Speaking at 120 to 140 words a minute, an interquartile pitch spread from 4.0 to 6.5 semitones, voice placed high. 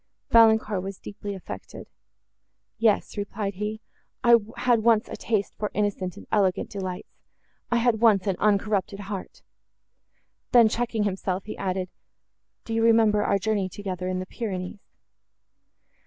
No: slow, 135 wpm; narrow, 2.5 semitones; high, 205 Hz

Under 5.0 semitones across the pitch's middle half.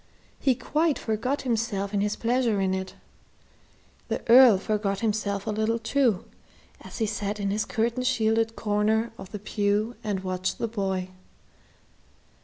Yes: narrow, 2.5 semitones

